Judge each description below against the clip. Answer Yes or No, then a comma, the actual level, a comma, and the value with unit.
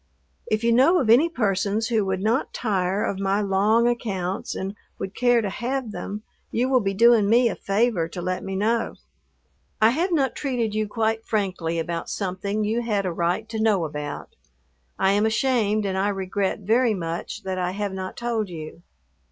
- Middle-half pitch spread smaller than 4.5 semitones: Yes, average, 3.4 semitones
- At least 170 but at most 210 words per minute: Yes, average, 190 wpm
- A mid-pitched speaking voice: No, high, 210 Hz